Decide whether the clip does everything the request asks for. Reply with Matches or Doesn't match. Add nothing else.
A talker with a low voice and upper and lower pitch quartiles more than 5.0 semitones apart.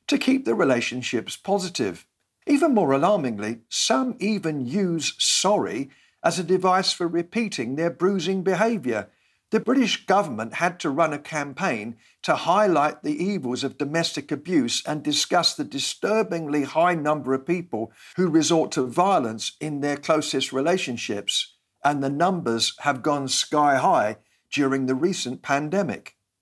Doesn't match